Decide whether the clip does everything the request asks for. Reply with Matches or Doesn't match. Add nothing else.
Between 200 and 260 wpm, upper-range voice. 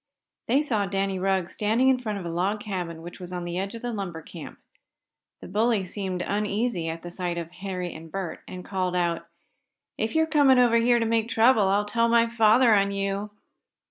Matches